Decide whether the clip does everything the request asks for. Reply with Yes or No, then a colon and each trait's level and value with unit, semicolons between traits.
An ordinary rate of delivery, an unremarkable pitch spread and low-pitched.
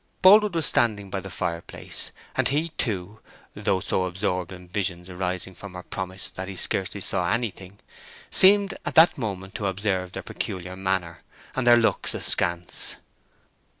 Yes: average, 160 wpm; average, 3.4 semitones; very low, 95 Hz